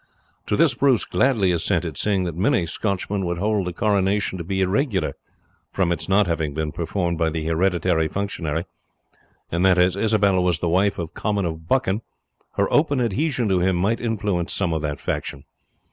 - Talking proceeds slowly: No, average, 180 wpm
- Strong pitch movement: No, average, 3.4 semitones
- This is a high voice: No, very low, 95 Hz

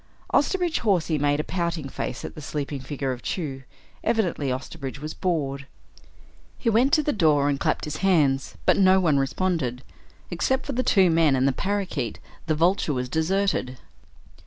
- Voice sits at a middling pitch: Yes, medium, 155 Hz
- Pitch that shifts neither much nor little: No, wide, 5.7 semitones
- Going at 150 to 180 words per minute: Yes, average, 170 wpm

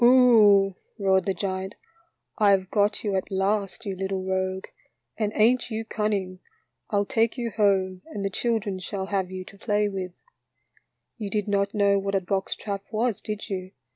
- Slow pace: No, average, 195 wpm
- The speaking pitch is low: No, high, 200 Hz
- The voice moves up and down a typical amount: No, narrow, 1.9 semitones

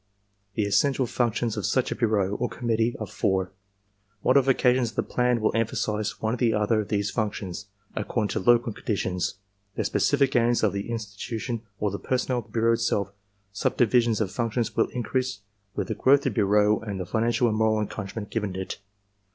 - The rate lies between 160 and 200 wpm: Yes, average, 190 wpm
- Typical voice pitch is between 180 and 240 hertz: No, low, 110 Hz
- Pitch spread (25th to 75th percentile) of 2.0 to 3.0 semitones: Yes, narrow, 2.6 semitones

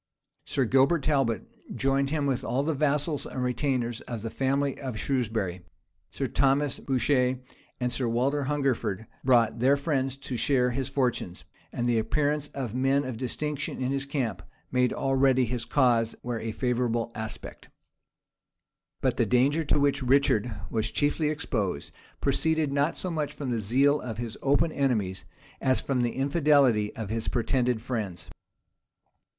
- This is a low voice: Yes, low, 130 Hz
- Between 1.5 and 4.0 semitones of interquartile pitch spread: Yes, average, 3.1 semitones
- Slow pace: No, average, 155 wpm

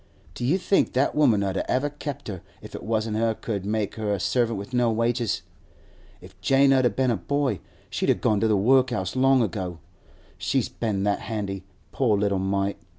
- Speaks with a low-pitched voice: Yes, low, 110 Hz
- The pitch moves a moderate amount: Yes, average, 4.3 semitones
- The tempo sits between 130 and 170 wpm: No, average, 200 wpm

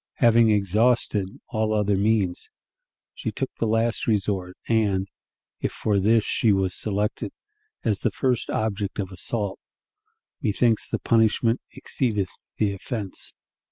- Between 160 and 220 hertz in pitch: No, low, 105 Hz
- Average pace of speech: No, slow, 125 wpm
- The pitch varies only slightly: Yes, narrow, 2.3 semitones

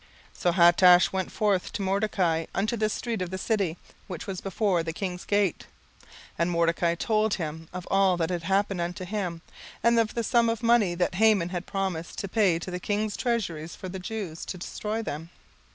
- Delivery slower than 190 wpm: No, fast, 205 wpm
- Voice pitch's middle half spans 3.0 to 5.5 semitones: Yes, average, 3.5 semitones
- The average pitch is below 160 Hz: No, medium, 185 Hz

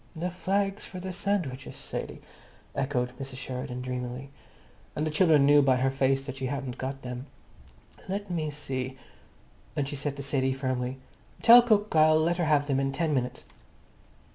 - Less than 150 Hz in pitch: Yes, medium, 140 Hz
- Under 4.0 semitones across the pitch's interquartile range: Yes, average, 3.5 semitones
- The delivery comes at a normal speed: Yes, average, 170 wpm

